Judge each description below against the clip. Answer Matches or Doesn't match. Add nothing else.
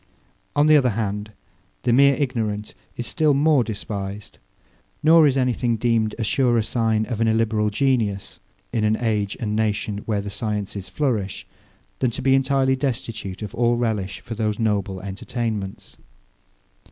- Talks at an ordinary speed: Matches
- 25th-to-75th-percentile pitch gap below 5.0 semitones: Matches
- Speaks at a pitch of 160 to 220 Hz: Doesn't match